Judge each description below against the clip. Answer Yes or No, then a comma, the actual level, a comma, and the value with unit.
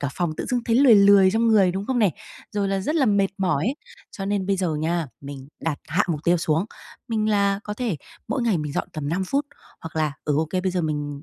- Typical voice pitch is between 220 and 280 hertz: No, high, 190 Hz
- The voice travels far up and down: No, average, 4.9 semitones